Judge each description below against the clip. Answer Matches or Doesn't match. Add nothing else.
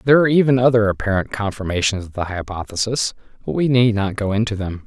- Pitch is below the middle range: Matches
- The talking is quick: Doesn't match